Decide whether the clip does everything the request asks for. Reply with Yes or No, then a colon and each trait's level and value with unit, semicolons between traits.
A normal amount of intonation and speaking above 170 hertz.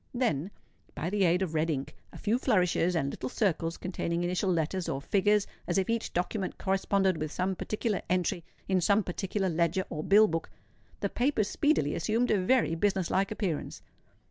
Yes: average, 3.6 semitones; medium, 185 Hz